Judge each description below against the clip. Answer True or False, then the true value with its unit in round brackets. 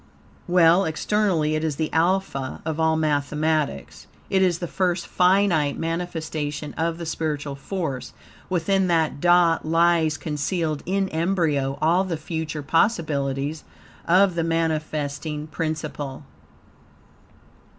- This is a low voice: False (160 Hz)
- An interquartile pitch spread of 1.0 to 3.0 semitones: True (2.5 semitones)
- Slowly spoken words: True (115 wpm)